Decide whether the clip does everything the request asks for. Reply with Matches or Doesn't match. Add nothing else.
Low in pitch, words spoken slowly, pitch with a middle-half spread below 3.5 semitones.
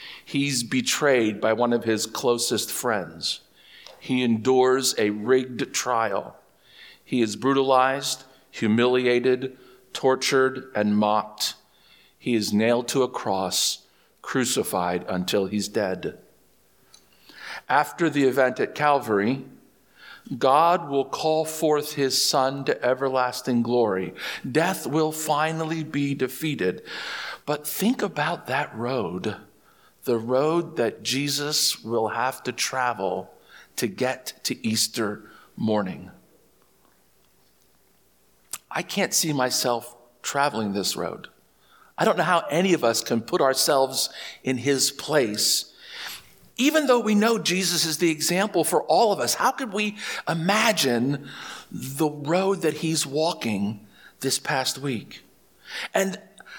Doesn't match